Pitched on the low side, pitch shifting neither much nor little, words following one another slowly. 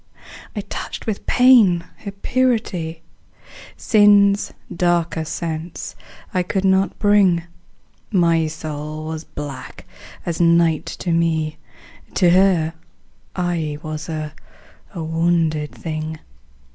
No: medium, 170 Hz; average, 3.2 semitones; slow, 100 wpm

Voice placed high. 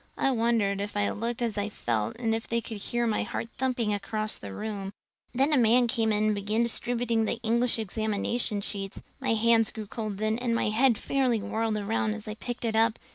Yes: high, 225 Hz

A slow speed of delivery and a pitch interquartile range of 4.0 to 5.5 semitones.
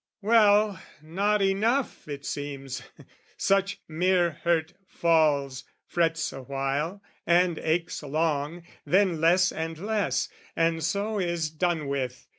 Yes: slow, 110 wpm; average, 4.3 semitones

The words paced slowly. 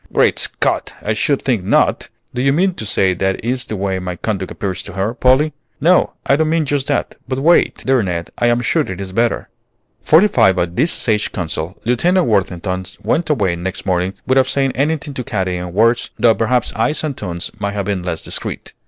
No: fast, 205 wpm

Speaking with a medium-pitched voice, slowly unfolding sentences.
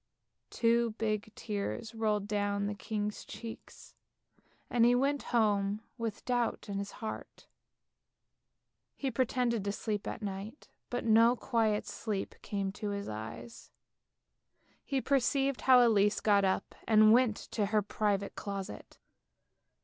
No: high, 215 Hz; slow, 130 wpm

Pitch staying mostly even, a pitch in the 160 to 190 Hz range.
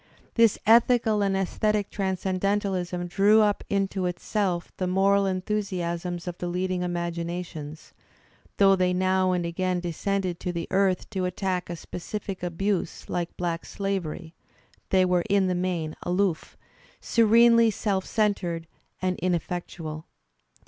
Yes: narrow, 2.1 semitones; medium, 185 Hz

